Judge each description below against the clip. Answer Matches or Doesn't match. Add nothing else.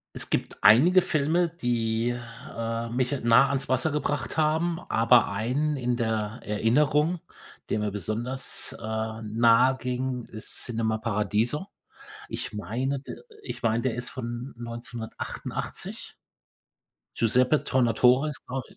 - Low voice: Matches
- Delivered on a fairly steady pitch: Doesn't match